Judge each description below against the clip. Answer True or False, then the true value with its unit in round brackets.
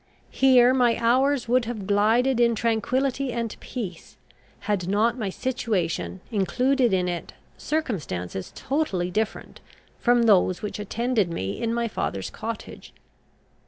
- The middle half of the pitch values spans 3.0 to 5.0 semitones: True (4.4 semitones)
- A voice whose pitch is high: True (230 Hz)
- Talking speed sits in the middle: False (125 wpm)